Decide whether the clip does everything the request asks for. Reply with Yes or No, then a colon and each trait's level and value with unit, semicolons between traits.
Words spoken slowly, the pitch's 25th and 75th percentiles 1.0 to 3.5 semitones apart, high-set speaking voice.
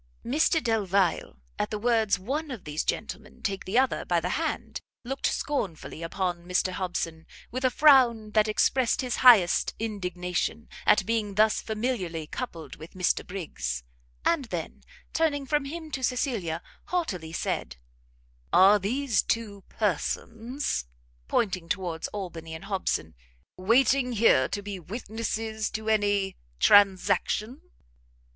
No: slow, 130 wpm; average, 5.2 semitones; high, 210 Hz